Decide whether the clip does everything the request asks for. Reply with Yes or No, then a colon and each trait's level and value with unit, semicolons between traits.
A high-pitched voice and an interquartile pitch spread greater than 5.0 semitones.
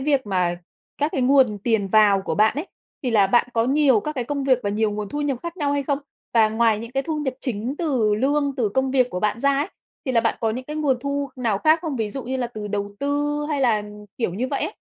No: very high, 255 Hz; average, 4.6 semitones